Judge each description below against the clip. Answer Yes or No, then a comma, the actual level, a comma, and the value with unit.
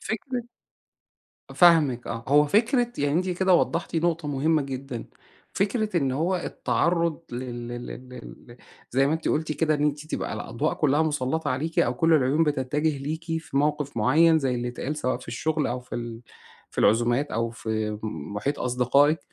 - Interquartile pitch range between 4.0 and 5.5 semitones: Yes, average, 4.5 semitones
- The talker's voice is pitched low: No, medium, 145 Hz